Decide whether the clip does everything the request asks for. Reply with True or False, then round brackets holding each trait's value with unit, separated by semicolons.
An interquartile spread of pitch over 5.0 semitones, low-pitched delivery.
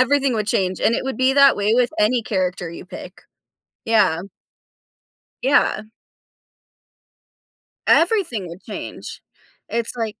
False (5.4 semitones; 225 Hz)